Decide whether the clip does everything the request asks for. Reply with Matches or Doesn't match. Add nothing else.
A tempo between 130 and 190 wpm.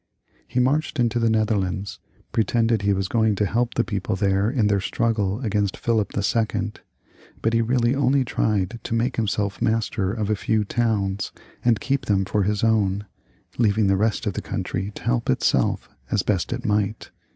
Matches